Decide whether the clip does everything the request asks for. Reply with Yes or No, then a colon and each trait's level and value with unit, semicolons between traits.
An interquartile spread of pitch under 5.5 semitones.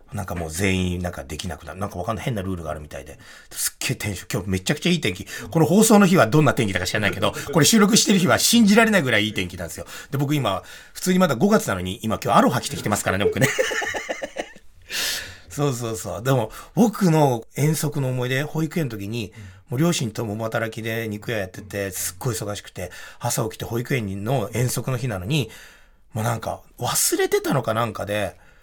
No: wide, 7.1 semitones